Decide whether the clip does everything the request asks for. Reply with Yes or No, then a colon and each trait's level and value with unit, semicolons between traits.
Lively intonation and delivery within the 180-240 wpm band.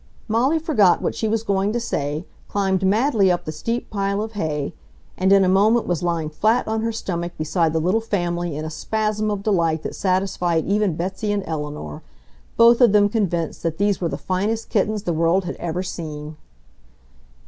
No: average, 4.3 semitones; average, 190 wpm